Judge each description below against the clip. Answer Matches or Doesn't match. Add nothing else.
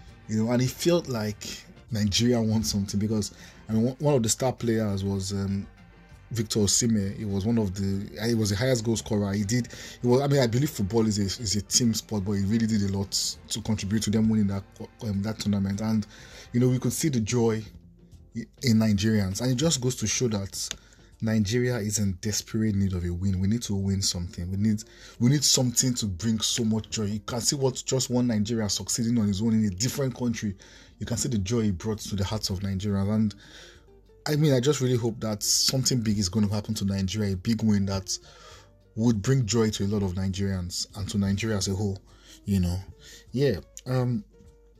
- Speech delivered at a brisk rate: Matches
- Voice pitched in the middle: Doesn't match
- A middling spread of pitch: Matches